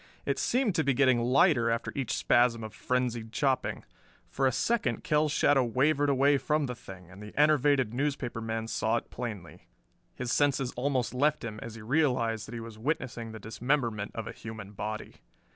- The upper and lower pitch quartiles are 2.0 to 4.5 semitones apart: Yes, average, 3.8 semitones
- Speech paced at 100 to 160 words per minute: No, average, 185 wpm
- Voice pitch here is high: No, low, 125 Hz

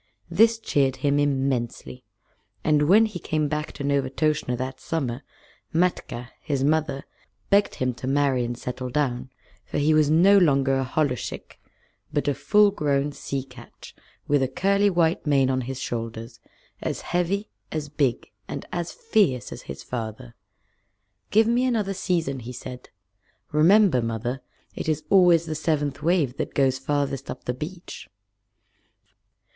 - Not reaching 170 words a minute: Yes, average, 150 wpm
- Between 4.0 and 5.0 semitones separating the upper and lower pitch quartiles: Yes, average, 4.4 semitones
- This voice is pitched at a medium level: Yes, medium, 145 Hz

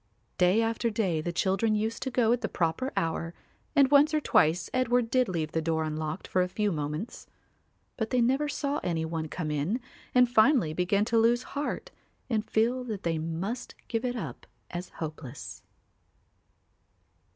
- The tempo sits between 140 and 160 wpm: No, average, 175 wpm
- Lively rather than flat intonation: Yes, wide, 7.0 semitones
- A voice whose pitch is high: Yes, high, 210 Hz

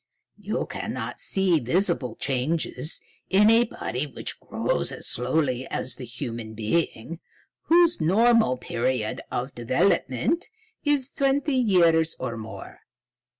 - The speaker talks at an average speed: No, slow, 115 wpm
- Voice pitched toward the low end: No, medium, 155 Hz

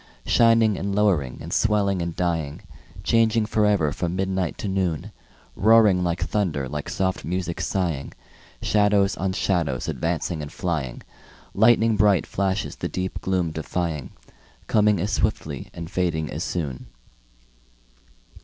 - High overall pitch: No, very low, 95 Hz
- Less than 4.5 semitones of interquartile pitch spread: Yes, average, 3.8 semitones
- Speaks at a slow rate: Yes, slow, 130 wpm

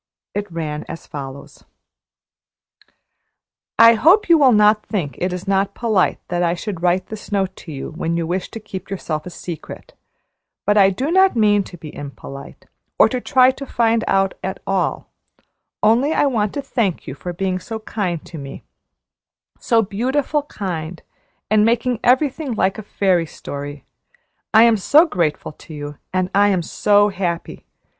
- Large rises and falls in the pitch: No, average, 4.9 semitones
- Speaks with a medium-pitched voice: No, high, 195 Hz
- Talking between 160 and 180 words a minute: Yes, average, 170 wpm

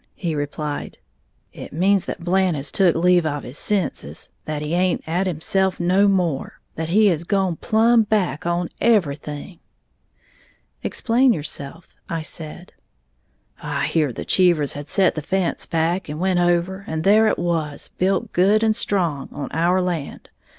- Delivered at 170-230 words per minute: No, average, 155 wpm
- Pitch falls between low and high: Yes, medium, 175 Hz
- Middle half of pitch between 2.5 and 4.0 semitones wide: Yes, average, 3.6 semitones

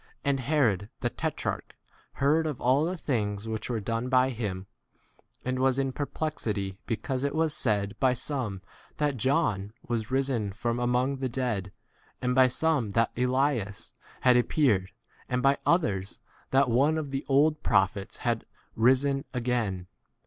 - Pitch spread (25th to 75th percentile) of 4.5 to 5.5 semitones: No, average, 4.1 semitones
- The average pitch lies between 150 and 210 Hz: No, low, 125 Hz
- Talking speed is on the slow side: No, average, 155 wpm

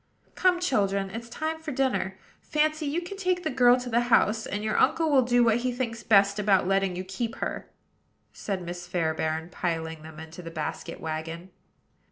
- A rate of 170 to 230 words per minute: Yes, average, 190 wpm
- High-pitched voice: Yes, high, 215 Hz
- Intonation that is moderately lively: No, wide, 6.5 semitones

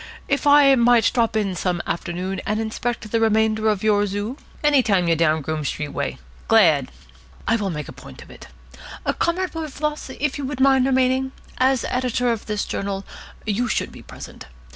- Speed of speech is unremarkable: Yes, average, 185 wpm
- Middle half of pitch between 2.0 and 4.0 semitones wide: No, average, 5.0 semitones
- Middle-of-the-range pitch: No, high, 225 Hz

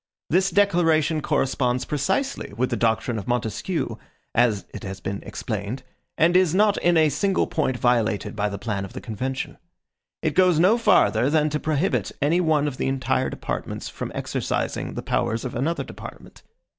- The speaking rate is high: No, average, 170 wpm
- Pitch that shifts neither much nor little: No, wide, 6.3 semitones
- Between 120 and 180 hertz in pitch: Yes, medium, 140 Hz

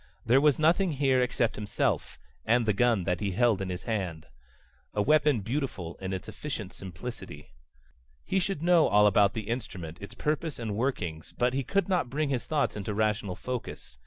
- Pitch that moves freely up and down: Yes, wide, 6.1 semitones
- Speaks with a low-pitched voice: Yes, low, 115 Hz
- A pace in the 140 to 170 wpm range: No, average, 185 wpm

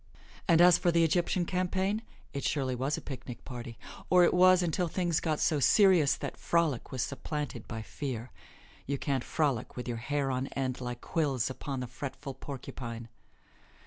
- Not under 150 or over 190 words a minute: Yes, average, 175 wpm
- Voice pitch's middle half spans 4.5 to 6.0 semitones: Yes, average, 5.0 semitones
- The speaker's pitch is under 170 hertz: Yes, medium, 140 Hz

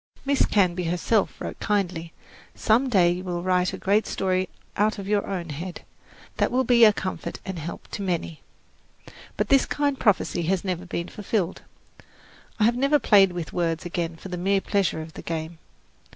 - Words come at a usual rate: Yes, average, 180 wpm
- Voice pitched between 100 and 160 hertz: No, medium, 185 Hz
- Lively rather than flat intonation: No, average, 3.4 semitones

